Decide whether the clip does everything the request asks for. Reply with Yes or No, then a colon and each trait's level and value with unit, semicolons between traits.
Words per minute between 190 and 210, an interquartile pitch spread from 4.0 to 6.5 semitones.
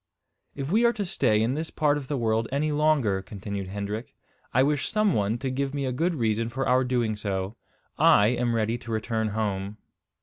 Yes: fast, 205 wpm; average, 4.9 semitones